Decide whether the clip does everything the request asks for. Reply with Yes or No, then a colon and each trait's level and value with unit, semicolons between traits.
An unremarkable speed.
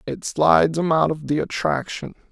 Yes: average, 180 wpm